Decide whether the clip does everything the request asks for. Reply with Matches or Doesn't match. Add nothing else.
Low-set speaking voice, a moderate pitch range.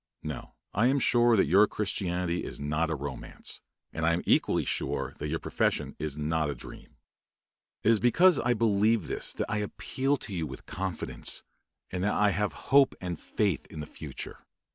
Doesn't match